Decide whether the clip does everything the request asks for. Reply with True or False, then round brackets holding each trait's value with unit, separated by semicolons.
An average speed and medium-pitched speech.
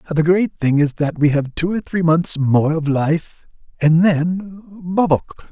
True (175 wpm; 165 Hz)